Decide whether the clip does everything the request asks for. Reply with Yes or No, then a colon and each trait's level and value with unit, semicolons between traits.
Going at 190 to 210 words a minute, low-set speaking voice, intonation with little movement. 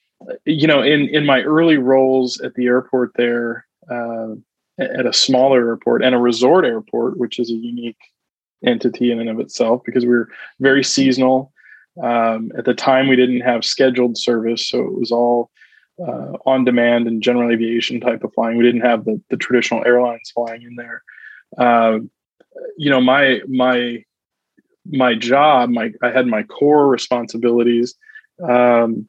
No: average, 165 wpm; low, 125 Hz; narrow, 2.0 semitones